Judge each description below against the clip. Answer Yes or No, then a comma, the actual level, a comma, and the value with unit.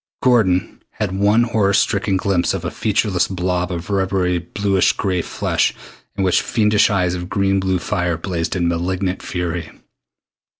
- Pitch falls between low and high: No, very low, 95 Hz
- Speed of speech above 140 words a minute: Yes, average, 155 wpm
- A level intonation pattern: Yes, narrow, 2.2 semitones